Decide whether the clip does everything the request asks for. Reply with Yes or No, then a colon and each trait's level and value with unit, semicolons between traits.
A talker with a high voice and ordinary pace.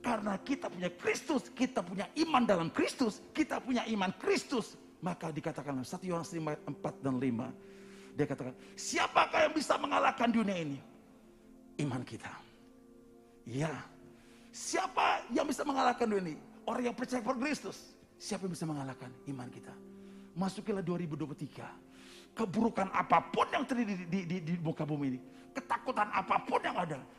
No: high, 195 Hz; fast, 150 wpm